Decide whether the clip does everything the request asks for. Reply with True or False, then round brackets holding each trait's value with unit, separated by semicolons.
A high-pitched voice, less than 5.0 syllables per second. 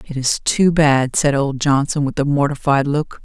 False (140 Hz; 4.5 syllables/s)